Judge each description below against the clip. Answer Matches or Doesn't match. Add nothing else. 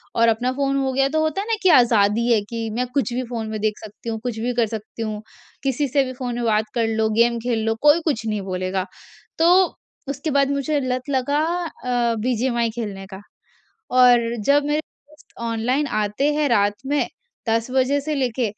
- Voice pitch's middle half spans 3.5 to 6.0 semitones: Matches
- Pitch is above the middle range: Matches